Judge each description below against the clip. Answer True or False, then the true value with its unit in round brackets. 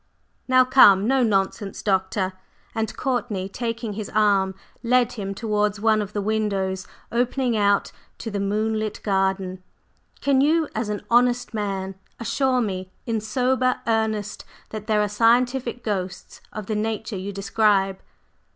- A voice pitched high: True (215 Hz)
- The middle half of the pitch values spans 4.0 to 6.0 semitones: False (3.1 semitones)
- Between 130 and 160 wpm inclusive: True (140 wpm)